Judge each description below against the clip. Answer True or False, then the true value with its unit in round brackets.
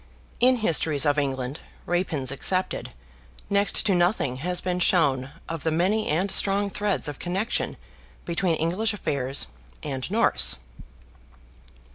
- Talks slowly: True (125 wpm)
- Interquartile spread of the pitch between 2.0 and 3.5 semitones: False (5.5 semitones)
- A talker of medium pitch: True (175 Hz)